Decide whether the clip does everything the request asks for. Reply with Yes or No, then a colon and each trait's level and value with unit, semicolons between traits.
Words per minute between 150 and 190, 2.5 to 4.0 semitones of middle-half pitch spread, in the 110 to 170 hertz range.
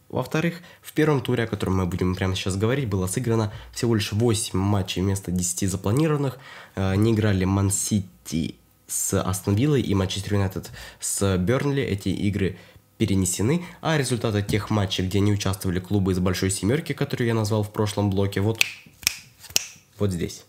No: fast, 160 wpm; average, 3.3 semitones; low, 100 Hz